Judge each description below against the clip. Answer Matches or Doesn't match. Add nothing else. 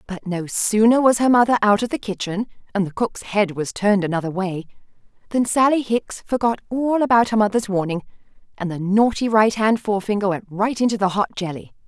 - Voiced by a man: Doesn't match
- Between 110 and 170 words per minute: Doesn't match